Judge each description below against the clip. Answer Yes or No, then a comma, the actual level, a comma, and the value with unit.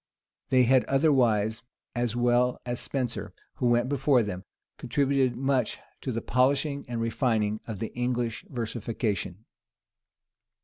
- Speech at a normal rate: No, slow, 125 wpm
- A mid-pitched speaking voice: No, low, 120 Hz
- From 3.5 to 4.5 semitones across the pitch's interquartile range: No, narrow, 2.4 semitones